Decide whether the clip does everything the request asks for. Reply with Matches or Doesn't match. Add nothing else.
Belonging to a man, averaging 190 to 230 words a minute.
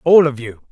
Doesn't match